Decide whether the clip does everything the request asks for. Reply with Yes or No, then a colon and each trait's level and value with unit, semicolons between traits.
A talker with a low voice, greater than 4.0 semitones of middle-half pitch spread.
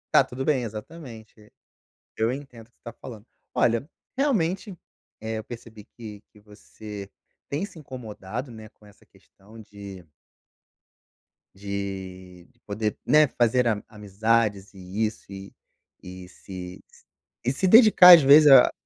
Yes: low, 110 Hz; average, 4.5 semitones